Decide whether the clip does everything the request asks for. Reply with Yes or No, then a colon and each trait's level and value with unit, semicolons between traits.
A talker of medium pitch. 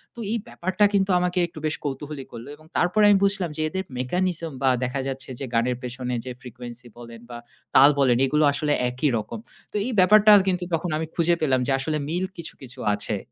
Yes: medium, 150 Hz